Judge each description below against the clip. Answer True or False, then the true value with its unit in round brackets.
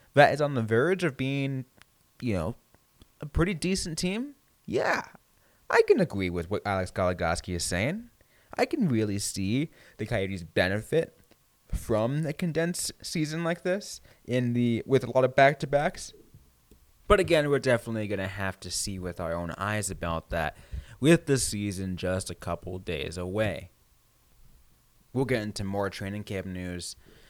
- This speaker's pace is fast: False (165 wpm)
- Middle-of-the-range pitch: False (110 Hz)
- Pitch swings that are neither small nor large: False (7.5 semitones)